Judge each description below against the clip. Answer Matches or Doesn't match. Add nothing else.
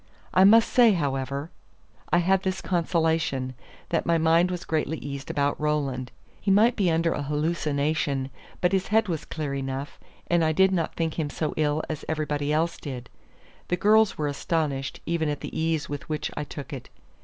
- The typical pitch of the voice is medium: Matches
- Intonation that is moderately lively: Matches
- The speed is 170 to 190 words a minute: Matches